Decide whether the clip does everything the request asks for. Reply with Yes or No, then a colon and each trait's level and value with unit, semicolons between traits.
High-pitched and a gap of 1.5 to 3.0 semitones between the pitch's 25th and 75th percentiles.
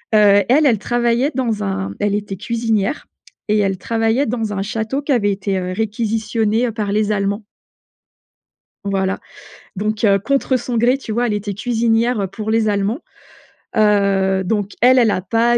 Yes: high, 215 Hz; average, 2.7 semitones